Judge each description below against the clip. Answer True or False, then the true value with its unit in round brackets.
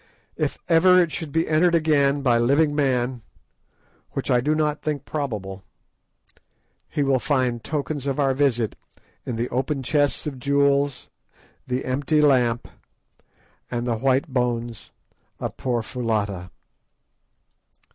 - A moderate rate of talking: False (130 wpm)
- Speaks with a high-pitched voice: False (135 Hz)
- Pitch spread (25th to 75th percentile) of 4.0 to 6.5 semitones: False (3.4 semitones)